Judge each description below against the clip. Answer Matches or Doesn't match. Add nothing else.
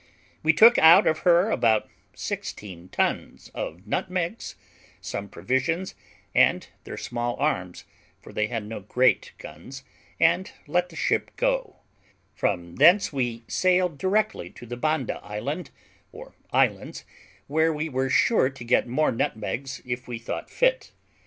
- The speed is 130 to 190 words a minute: Matches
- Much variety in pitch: Matches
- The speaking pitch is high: Doesn't match